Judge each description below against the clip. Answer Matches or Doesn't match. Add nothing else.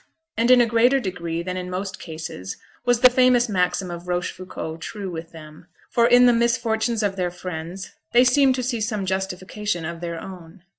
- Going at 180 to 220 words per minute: Matches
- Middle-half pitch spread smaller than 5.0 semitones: Doesn't match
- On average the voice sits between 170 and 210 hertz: Matches